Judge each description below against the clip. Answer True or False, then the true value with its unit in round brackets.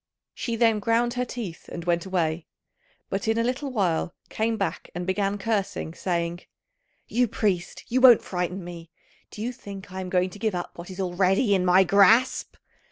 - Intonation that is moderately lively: True (4.2 semitones)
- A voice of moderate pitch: False (195 Hz)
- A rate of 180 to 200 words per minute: True (185 wpm)